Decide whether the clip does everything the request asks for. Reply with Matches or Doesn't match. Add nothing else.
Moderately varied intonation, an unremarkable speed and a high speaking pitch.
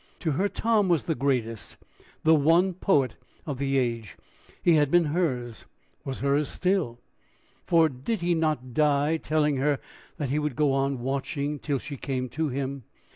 Doesn't match